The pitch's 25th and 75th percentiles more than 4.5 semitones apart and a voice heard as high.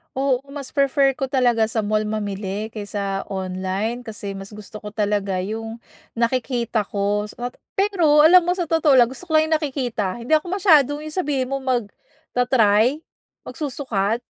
Yes: wide, 5.5 semitones; high, 240 Hz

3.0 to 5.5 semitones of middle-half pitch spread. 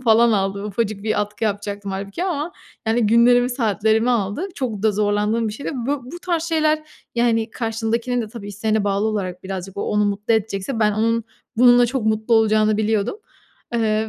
No: narrow, 2.5 semitones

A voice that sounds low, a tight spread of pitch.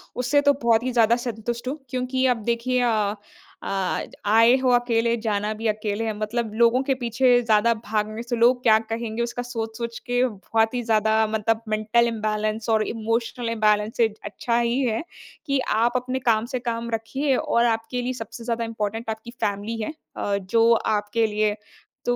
No: high, 230 Hz; narrow, 1.8 semitones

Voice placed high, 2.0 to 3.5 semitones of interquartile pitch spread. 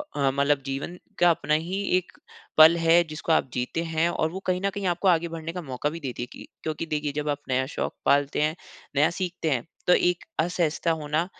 No: medium, 160 Hz; average, 2.8 semitones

